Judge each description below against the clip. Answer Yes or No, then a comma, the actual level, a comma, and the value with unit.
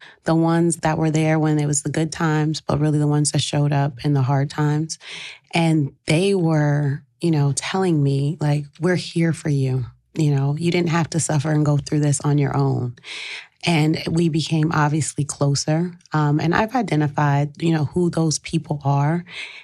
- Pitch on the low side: No, medium, 150 Hz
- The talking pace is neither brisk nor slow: Yes, average, 195 wpm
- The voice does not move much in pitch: Yes, narrow, 2.2 semitones